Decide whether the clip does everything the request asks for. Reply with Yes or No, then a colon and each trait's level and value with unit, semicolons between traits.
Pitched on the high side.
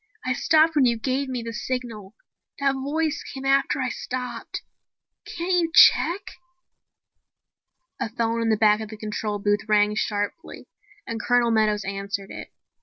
Yes: high, 235 Hz